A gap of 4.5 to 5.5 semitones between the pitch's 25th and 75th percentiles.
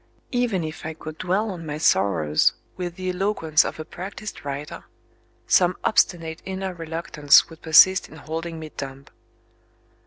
No: average, 3.2 semitones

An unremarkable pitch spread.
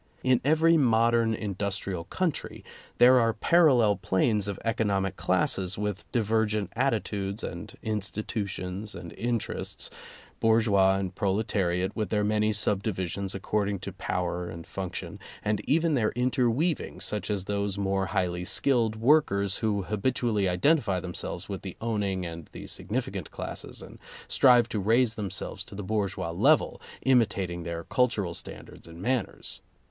Yes: average, 3.3 semitones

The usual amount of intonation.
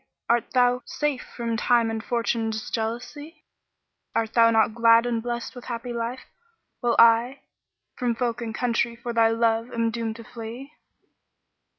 No: narrow, 1.2 semitones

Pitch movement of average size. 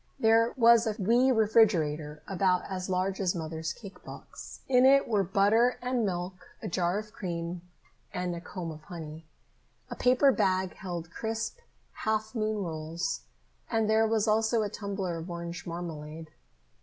Yes: average, 4.5 semitones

